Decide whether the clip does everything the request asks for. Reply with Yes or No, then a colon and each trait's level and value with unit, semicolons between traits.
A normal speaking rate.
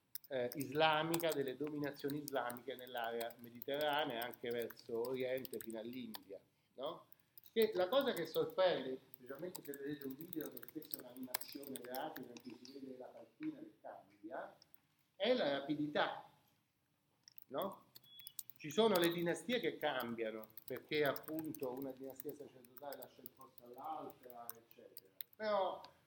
Yes: average, 125 wpm